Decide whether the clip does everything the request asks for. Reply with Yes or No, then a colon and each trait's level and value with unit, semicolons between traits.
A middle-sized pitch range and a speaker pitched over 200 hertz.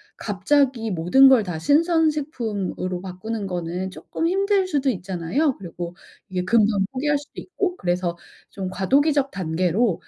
No: wide, 7.9 semitones; high, 210 Hz